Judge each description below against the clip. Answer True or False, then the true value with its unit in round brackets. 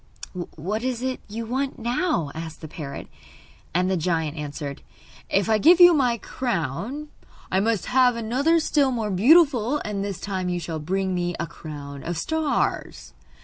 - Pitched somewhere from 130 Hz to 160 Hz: False (205 Hz)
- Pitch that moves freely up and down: True (7.4 semitones)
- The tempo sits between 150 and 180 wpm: True (165 wpm)